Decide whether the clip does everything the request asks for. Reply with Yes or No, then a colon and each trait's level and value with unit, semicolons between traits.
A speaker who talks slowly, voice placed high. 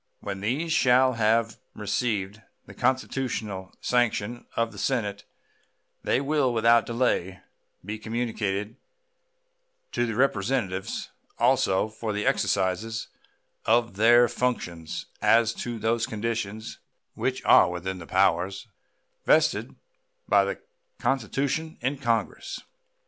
No: slow, 110 wpm; low, 115 Hz